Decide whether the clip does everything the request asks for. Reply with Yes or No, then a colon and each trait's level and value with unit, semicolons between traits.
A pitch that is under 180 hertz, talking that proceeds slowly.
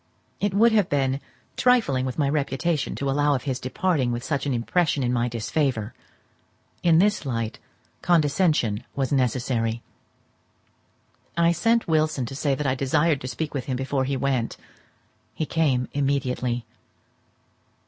No: medium, 140 Hz; average, 150 wpm